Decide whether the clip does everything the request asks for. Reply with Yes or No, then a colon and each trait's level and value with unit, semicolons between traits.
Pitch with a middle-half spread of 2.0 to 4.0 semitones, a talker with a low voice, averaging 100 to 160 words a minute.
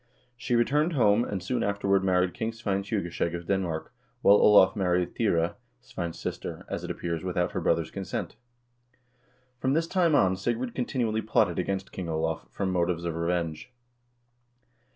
No: average, 4.9 semitones; very low, 95 Hz; average, 155 wpm